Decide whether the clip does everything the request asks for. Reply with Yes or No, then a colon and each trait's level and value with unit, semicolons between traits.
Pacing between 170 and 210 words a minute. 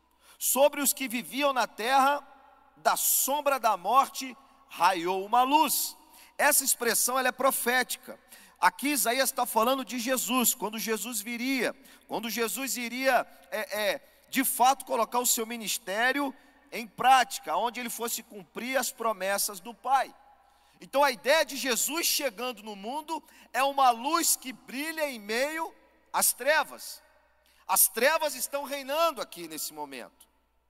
No: average, 140 wpm